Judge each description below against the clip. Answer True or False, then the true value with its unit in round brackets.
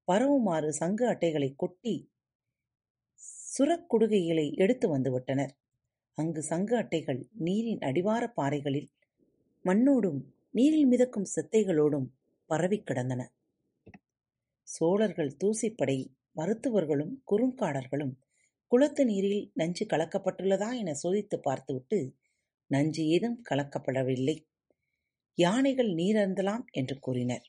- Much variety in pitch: True (7.6 semitones)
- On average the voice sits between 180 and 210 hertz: False (165 Hz)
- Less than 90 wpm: True (80 wpm)